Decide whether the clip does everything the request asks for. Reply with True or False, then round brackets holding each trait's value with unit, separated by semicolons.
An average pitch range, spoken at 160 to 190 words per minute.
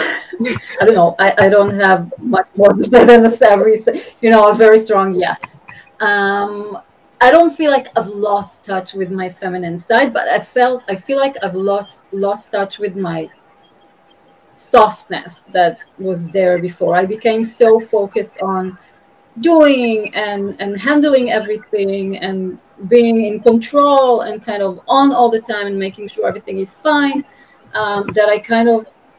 True (3.2 semitones; 165 wpm)